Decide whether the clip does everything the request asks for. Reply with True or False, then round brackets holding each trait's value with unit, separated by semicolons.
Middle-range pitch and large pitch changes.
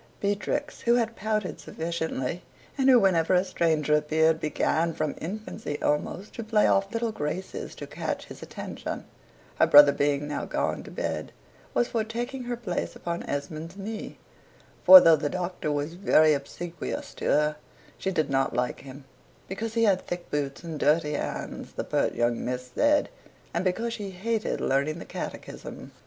True (170 Hz; 6.3 semitones)